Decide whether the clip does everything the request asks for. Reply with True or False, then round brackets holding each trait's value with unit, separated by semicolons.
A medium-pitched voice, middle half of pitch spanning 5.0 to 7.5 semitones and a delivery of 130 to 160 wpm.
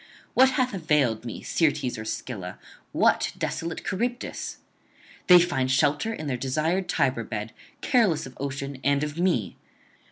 True (145 Hz; 5.5 semitones; 140 wpm)